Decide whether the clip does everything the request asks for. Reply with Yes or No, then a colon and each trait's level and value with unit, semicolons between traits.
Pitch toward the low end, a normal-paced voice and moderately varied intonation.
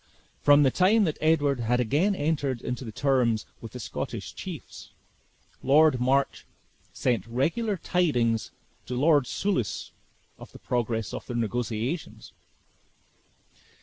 No: low, 130 Hz; slow, 120 wpm; average, 4.8 semitones